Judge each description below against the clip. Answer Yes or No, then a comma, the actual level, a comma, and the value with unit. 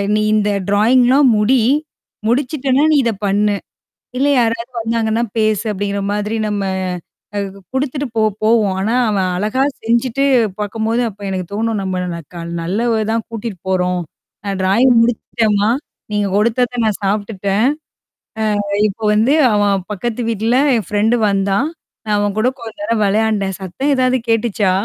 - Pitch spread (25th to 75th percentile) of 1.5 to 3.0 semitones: Yes, average, 2.7 semitones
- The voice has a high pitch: Yes, high, 215 Hz